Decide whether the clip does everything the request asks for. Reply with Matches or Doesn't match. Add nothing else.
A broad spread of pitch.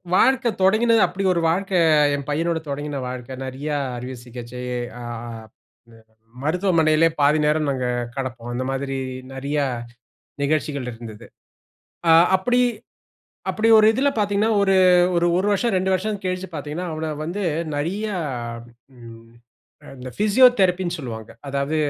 Matches